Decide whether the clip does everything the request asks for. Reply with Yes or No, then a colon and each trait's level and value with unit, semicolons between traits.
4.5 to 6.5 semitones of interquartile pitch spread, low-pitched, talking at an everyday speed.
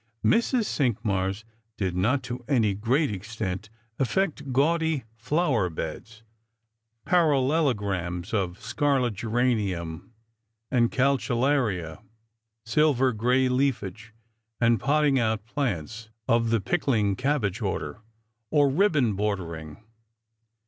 No: average, 5.2 semitones; low, 115 Hz; slow, 100 wpm